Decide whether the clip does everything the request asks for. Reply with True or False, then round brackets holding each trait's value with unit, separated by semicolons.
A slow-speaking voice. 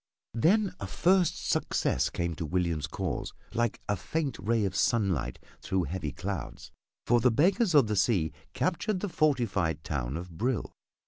False (155 wpm)